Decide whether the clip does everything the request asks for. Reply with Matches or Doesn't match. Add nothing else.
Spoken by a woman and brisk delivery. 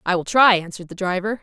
Matches